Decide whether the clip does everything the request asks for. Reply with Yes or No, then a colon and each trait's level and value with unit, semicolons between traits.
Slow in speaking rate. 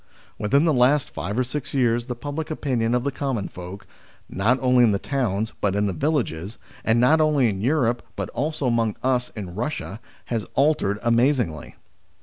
No: average, 180 wpm